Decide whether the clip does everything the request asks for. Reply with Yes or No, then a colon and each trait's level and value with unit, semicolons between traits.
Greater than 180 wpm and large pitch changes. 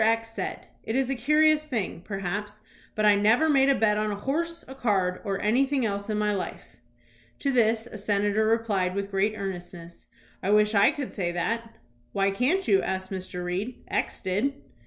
No: average, 190 wpm; average, 4.0 semitones